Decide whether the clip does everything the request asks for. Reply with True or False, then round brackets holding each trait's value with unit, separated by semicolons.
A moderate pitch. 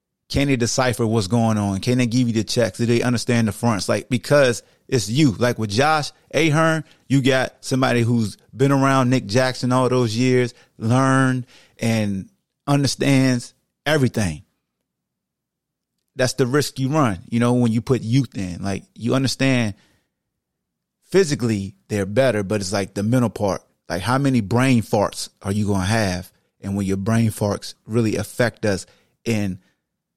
False (120 Hz)